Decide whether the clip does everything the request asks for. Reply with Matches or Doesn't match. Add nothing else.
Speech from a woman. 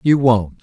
Doesn't match